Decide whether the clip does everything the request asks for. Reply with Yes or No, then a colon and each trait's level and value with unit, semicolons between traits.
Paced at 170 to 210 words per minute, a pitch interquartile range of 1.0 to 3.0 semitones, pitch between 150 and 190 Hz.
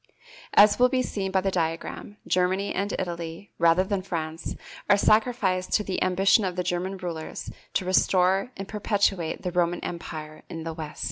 Yes: average, 175 wpm; average, 2.7 semitones; medium, 185 Hz